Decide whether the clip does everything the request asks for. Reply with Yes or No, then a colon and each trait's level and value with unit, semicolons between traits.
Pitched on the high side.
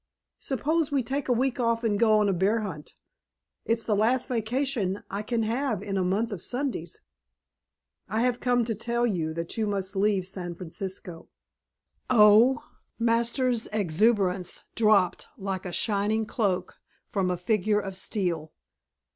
Yes: high, 215 Hz